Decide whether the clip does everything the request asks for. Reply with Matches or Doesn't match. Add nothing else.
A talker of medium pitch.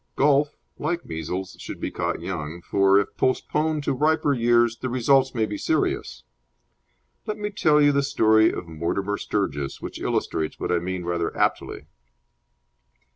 Doesn't match